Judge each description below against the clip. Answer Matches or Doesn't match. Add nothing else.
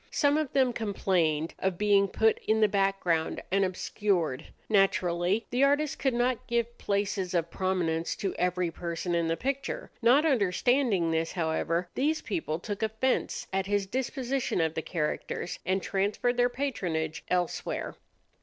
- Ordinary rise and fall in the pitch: Doesn't match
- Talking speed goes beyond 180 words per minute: Doesn't match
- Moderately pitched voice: Doesn't match